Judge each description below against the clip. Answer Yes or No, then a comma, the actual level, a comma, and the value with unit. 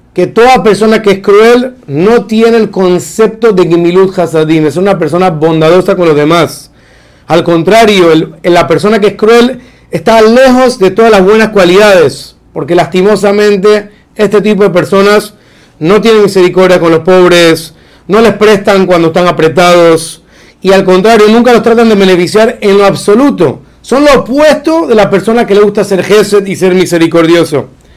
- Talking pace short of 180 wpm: Yes, average, 165 wpm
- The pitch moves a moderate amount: Yes, average, 4.1 semitones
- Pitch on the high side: Yes, high, 195 Hz